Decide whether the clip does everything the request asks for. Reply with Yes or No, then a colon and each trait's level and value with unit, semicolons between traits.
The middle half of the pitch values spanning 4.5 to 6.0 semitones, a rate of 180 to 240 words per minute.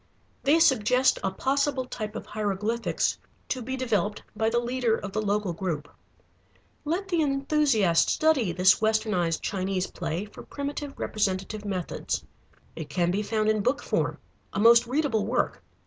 No: average, 5.0 semitones; average, 150 wpm